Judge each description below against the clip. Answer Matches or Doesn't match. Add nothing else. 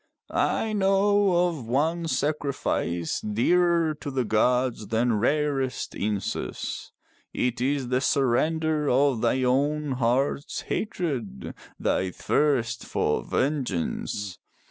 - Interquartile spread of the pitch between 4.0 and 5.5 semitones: Matches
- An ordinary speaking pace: Doesn't match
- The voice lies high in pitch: Doesn't match